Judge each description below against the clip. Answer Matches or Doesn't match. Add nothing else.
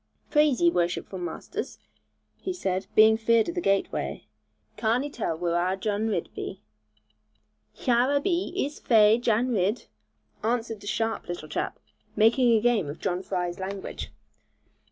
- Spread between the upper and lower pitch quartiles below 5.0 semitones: Matches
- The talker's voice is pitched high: Matches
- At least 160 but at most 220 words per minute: Doesn't match